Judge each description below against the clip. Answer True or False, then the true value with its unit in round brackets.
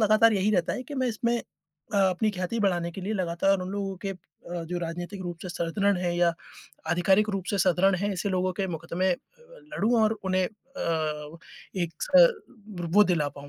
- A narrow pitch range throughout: False (3.3 semitones)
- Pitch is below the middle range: False (190 Hz)